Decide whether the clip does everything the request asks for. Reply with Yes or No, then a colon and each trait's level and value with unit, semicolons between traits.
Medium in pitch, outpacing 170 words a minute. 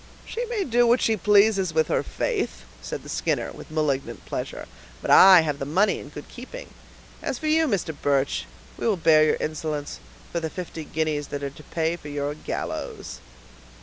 Yes: medium, 160 Hz; average, 190 wpm